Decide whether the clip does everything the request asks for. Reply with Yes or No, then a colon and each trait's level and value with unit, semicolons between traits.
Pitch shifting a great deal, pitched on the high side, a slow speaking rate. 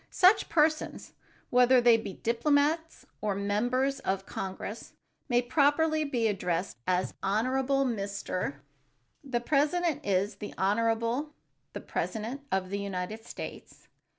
Yes: wide, 5.7 semitones; high, 235 Hz; slow, 125 wpm